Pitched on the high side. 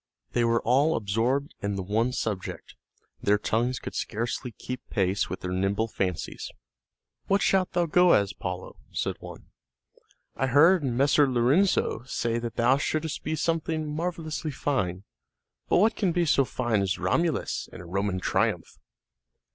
No: low, 125 Hz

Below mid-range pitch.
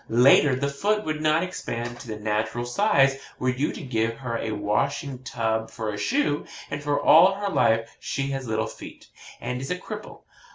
Yes: low, 130 Hz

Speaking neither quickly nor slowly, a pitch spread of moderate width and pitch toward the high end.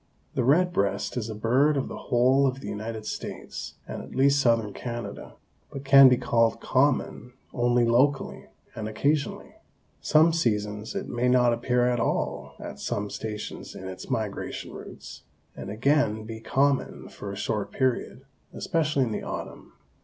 No: average, 160 wpm; average, 3.8 semitones; low, 120 Hz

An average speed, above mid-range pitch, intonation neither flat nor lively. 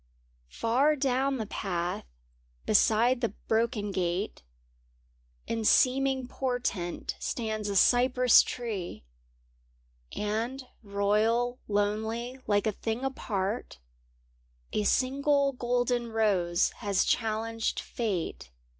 No: slow, 95 wpm; high, 225 Hz; average, 3.4 semitones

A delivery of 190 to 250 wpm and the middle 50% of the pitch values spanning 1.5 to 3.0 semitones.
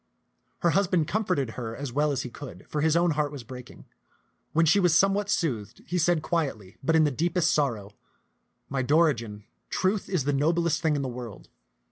No: fast, 205 wpm; average, 5.0 semitones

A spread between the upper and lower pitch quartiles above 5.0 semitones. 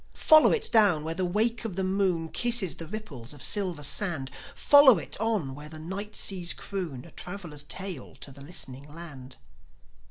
Yes: wide, 5.5 semitones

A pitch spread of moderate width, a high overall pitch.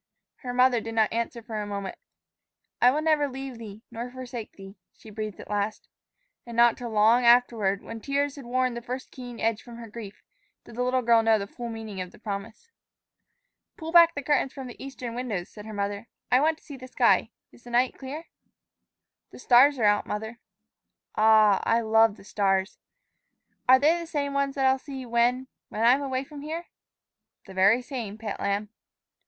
Yes: average, 3.4 semitones; high, 235 Hz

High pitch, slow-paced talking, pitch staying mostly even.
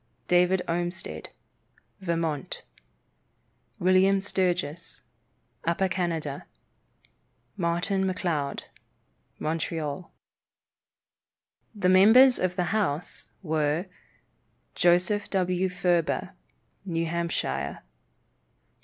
No: medium, 175 Hz; slow, 65 wpm; narrow, 2.2 semitones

